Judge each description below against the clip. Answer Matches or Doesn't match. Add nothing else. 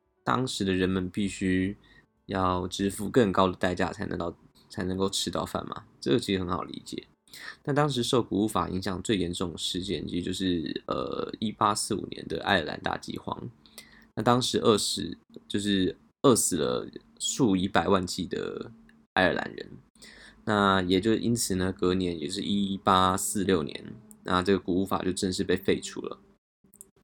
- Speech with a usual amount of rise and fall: Doesn't match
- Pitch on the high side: Doesn't match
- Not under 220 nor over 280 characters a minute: Matches